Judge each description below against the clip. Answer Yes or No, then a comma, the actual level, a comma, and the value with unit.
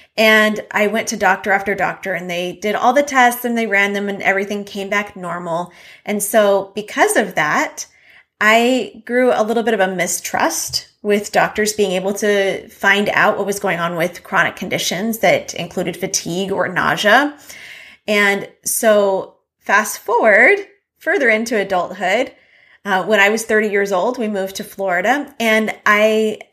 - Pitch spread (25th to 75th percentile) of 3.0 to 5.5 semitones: No, narrow, 2.4 semitones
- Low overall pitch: No, high, 205 Hz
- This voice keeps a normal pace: Yes, average, 165 wpm